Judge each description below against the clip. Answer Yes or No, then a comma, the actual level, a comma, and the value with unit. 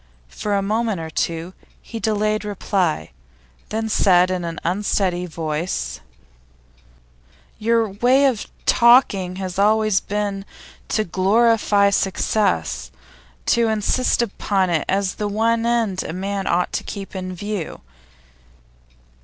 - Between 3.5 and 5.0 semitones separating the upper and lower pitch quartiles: No, average, 3.0 semitones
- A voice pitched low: No, high, 200 Hz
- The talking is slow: Yes, slow, 120 wpm